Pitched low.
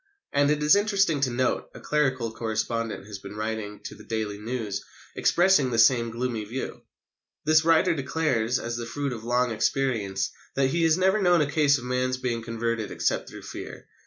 Yes: low, 125 Hz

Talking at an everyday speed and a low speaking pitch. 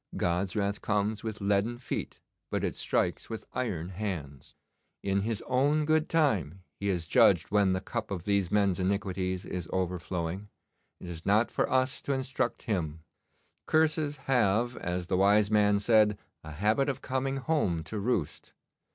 Yes: average, 160 wpm; low, 100 Hz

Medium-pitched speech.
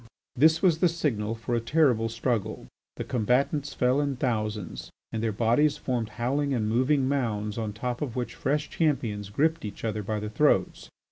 No: low, 120 Hz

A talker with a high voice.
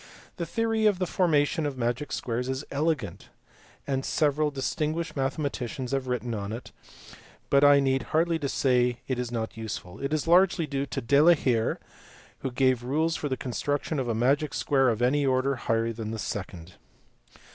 No: low, 135 Hz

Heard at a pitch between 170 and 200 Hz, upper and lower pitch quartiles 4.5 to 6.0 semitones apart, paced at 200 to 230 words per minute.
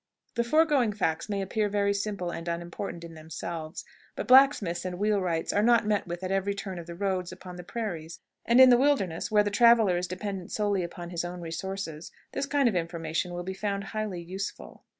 No: high, 190 Hz; average, 3.5 semitones; fast, 205 wpm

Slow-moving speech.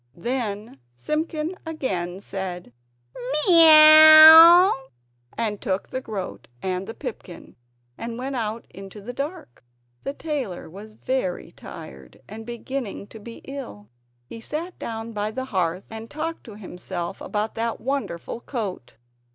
Yes: slow, 130 wpm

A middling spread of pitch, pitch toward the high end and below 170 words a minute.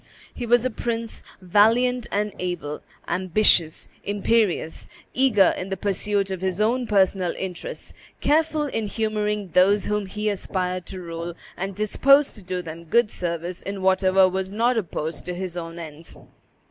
Yes: average, 3.1 semitones; high, 195 Hz; average, 155 wpm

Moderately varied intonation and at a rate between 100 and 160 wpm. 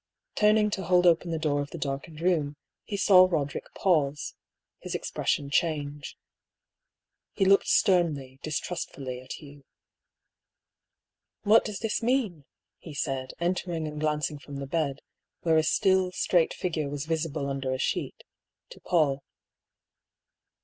Yes: average, 4.1 semitones; average, 140 wpm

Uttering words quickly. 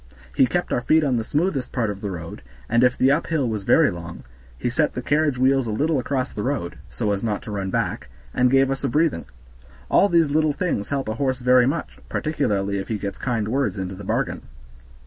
Yes: fast, 225 wpm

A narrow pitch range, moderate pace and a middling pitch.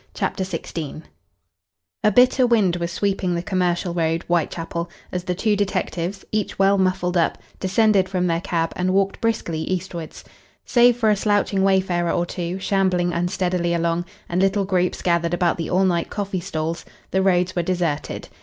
Yes: narrow, 2.2 semitones; average, 165 wpm; medium, 180 Hz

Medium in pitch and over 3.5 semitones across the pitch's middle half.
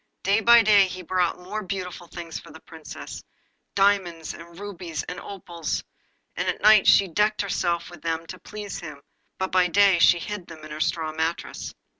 No: medium, 180 Hz; average, 3.2 semitones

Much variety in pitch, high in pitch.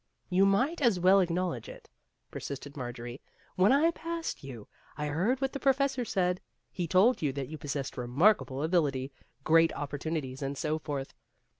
No: wide, 6.5 semitones; medium, 165 Hz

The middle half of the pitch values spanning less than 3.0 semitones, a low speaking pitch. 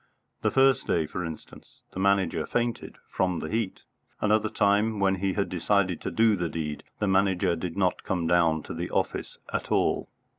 No: average, 3.4 semitones; very low, 95 Hz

